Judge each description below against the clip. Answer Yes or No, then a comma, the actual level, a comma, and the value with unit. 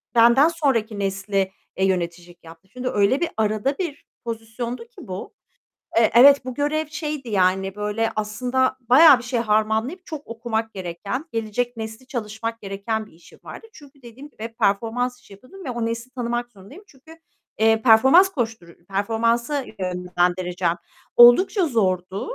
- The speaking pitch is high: Yes, high, 230 Hz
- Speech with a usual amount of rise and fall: Yes, average, 4.5 semitones